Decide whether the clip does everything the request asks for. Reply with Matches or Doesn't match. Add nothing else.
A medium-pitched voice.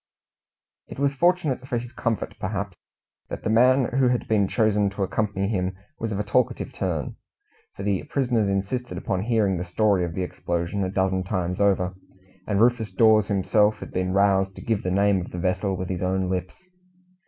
Doesn't match